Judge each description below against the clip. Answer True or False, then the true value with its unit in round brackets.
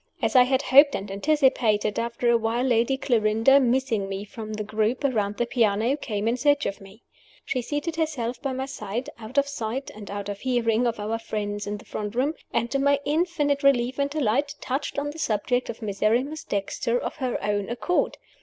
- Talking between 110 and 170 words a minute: False (200 wpm)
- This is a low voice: False (240 Hz)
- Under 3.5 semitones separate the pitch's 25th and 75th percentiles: False (4.5 semitones)